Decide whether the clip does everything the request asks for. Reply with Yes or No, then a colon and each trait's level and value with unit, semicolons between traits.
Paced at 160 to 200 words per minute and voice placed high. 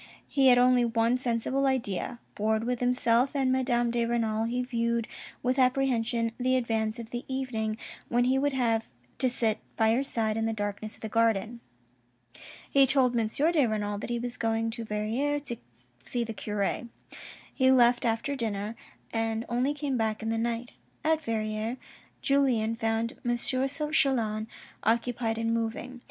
Yes: average, 165 wpm; high, 235 Hz